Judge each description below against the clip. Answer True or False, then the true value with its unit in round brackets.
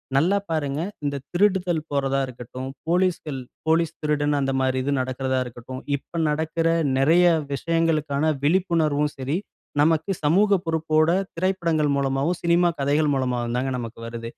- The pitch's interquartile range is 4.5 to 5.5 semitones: False (3.7 semitones)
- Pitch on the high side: False (150 Hz)